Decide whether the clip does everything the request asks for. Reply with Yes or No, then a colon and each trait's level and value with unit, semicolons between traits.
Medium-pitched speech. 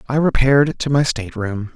No: low, 130 Hz